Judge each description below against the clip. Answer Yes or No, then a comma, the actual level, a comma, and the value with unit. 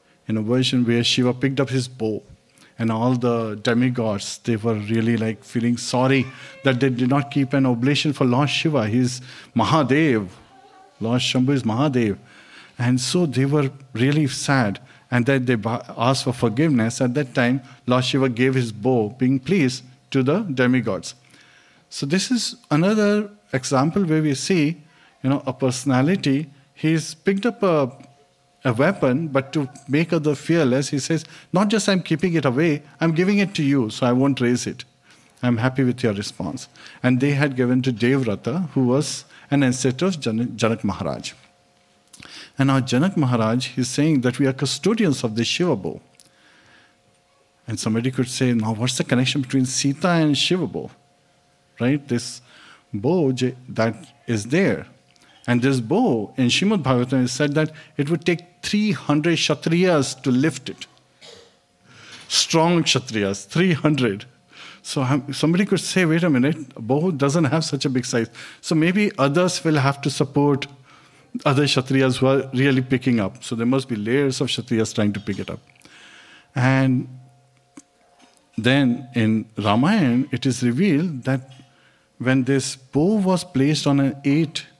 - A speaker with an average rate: Yes, average, 165 wpm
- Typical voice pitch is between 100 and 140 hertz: Yes, low, 135 Hz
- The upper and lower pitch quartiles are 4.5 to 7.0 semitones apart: No, average, 3.3 semitones